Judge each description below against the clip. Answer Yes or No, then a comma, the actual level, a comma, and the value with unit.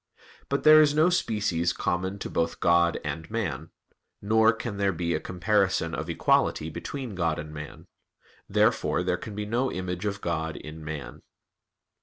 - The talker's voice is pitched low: Yes, very low, 90 Hz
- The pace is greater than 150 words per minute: Yes, average, 165 wpm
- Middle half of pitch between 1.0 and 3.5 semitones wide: No, average, 4.6 semitones